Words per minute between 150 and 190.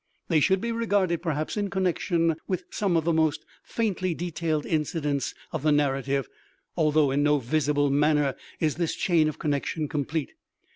Yes: average, 160 wpm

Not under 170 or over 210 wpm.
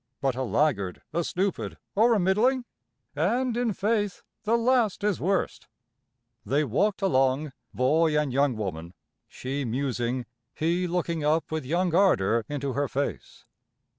No: average, 140 wpm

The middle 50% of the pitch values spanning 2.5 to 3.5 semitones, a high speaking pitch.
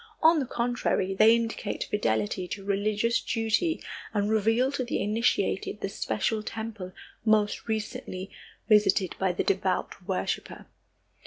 Yes: average, 2.9 semitones; high, 215 Hz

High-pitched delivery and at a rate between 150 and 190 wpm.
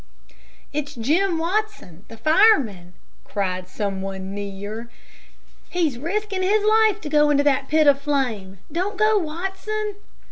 No: very high, 295 Hz; slow, 135 wpm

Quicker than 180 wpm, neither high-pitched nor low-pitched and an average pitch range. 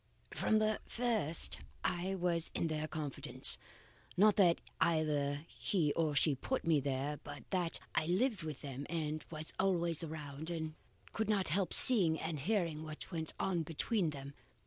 No: average, 160 wpm; medium, 160 Hz; average, 3.6 semitones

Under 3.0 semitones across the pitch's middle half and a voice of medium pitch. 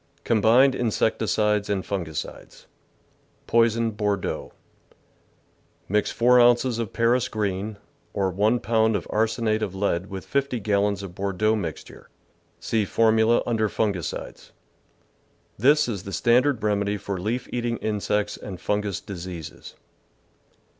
No: narrow, 2.6 semitones; low, 105 Hz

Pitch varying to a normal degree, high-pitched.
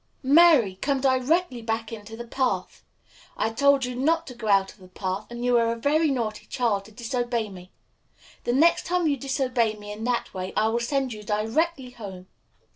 Yes: average, 4.0 semitones; high, 235 Hz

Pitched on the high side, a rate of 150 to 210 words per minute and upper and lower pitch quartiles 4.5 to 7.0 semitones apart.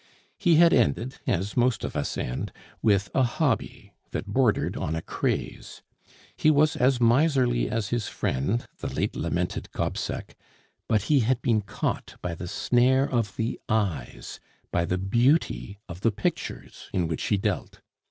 No: low, 115 Hz; average, 160 wpm; average, 5.3 semitones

